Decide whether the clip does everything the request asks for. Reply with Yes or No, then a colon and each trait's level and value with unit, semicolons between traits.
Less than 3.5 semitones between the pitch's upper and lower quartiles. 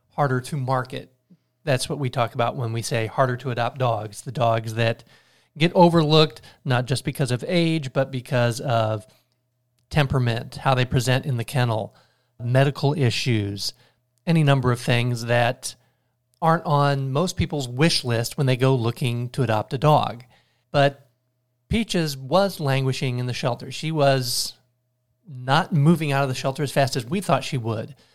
Yes: average, 2.7 semitones